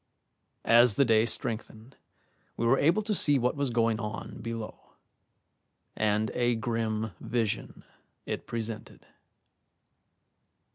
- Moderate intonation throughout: No, narrow, 2.0 semitones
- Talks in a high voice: No, low, 115 Hz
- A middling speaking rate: No, slow, 110 wpm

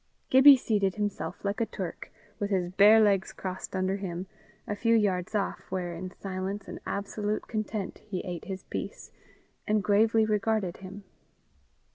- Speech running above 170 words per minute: No, average, 155 wpm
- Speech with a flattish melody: Yes, narrow, 2.2 semitones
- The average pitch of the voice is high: Yes, high, 200 Hz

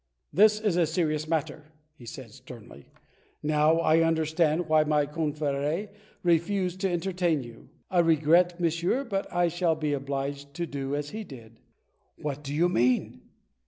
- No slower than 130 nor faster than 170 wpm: Yes, average, 155 wpm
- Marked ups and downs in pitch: No, average, 3.4 semitones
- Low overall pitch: No, medium, 155 Hz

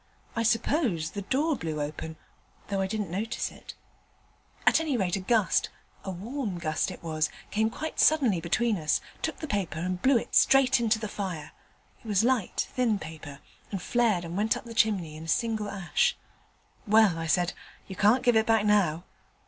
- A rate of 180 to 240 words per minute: Yes, average, 190 wpm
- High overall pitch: Yes, high, 205 Hz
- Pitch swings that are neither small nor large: Yes, average, 5.0 semitones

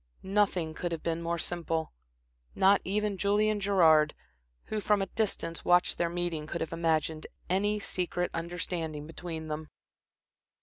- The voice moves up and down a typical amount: Yes, average, 3.2 semitones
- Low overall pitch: No, medium, 175 Hz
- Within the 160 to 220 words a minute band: No, average, 140 wpm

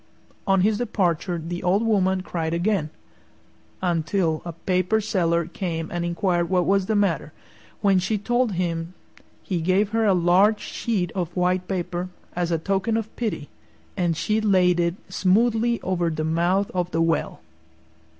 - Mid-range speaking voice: Yes, medium, 180 Hz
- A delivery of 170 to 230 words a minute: No, average, 160 wpm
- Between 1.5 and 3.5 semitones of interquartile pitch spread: Yes, average, 2.9 semitones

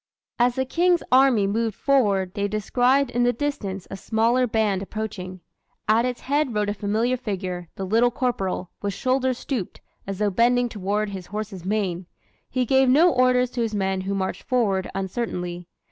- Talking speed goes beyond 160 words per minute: Yes, average, 175 wpm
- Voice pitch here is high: Yes, high, 215 Hz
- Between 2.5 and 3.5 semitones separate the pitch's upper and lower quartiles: No, average, 4.4 semitones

